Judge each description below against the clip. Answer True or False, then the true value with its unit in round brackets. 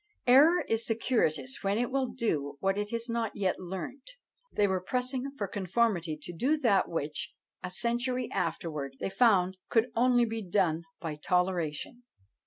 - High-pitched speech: True (205 Hz)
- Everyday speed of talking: True (160 wpm)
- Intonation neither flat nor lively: False (5.8 semitones)